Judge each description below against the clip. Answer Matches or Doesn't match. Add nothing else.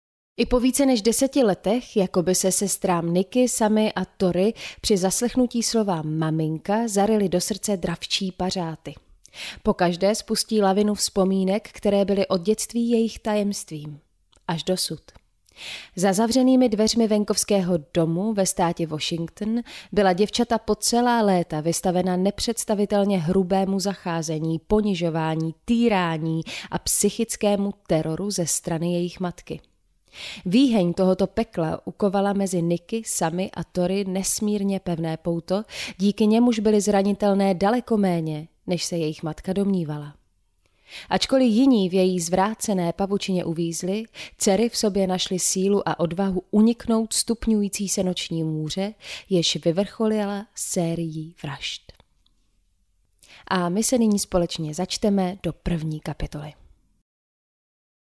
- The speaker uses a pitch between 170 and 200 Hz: Matches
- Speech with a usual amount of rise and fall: Matches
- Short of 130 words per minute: Matches